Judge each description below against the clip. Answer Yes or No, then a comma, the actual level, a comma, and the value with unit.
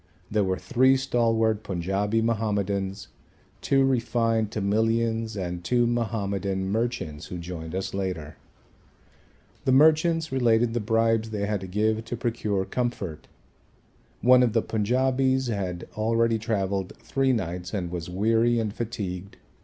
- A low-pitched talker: Yes, low, 110 Hz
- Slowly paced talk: Yes, slow, 130 wpm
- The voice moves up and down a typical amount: Yes, average, 3.5 semitones